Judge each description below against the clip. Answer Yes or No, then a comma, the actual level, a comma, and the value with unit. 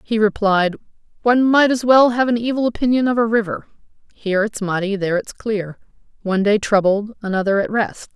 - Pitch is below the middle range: No, high, 215 Hz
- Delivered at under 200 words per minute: Yes, average, 185 wpm